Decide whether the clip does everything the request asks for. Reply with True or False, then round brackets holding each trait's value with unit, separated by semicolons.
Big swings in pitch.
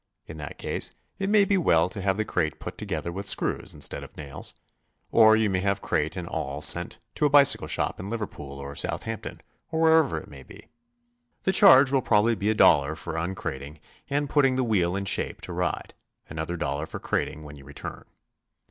True (8.8 semitones)